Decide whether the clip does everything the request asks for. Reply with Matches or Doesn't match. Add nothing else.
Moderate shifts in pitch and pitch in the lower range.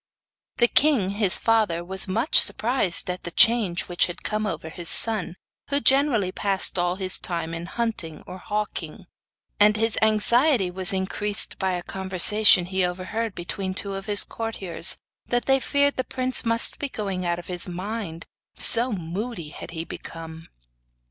Doesn't match